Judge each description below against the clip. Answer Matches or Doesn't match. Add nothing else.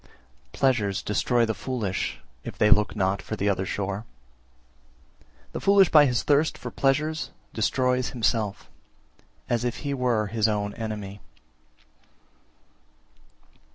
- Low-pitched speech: Matches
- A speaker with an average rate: Doesn't match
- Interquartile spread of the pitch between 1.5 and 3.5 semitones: Doesn't match